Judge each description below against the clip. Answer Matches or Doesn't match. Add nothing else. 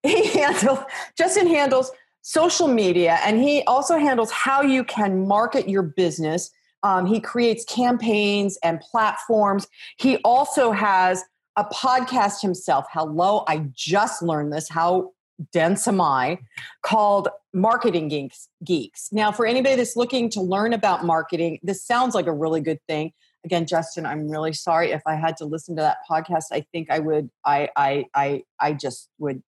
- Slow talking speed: Doesn't match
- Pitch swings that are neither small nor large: Doesn't match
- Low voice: Doesn't match